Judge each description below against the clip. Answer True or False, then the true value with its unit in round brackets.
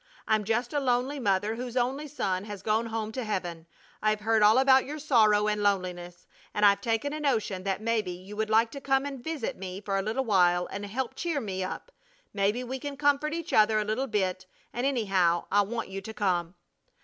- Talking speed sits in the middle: False (215 wpm)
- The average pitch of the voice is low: False (215 Hz)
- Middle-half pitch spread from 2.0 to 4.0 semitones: False (4.8 semitones)